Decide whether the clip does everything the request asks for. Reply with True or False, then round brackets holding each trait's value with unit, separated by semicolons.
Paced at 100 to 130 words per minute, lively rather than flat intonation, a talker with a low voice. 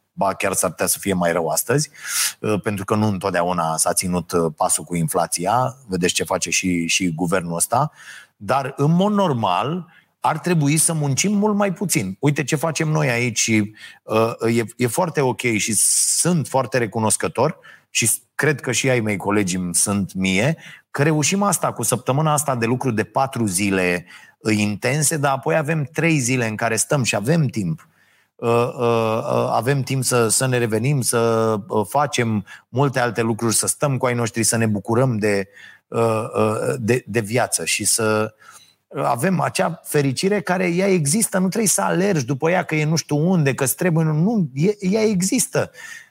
False (170 wpm; 6.3 semitones; 125 Hz)